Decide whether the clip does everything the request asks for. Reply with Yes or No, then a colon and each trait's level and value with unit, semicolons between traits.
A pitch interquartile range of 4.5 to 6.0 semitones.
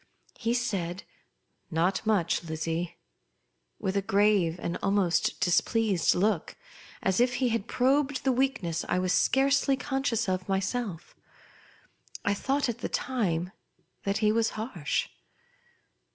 Yes: wide, 5.6 semitones